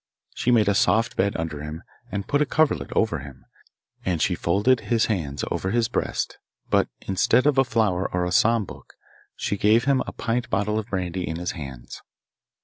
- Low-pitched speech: Yes, low, 100 Hz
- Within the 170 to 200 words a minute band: Yes, average, 195 wpm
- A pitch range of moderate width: Yes, average, 4.9 semitones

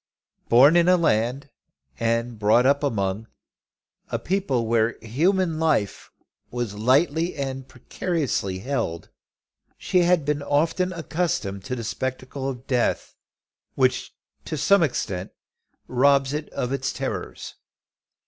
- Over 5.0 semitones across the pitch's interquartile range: Yes, wide, 5.4 semitones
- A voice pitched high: No, low, 135 Hz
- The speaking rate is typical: No, slow, 120 wpm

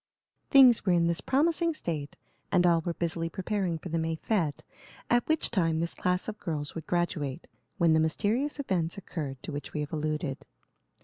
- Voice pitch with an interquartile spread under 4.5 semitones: Yes, average, 4.1 semitones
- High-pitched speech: No, medium, 170 Hz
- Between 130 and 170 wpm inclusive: No, average, 185 wpm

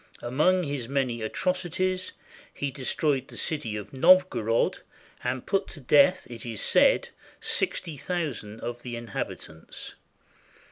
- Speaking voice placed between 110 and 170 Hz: Yes, low, 135 Hz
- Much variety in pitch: Yes, wide, 6.9 semitones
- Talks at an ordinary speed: No, slow, 125 wpm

